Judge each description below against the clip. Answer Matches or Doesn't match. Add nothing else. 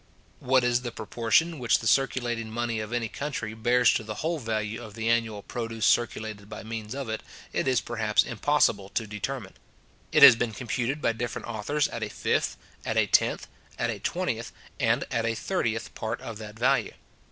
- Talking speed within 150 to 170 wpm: Doesn't match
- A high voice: Doesn't match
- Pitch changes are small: Matches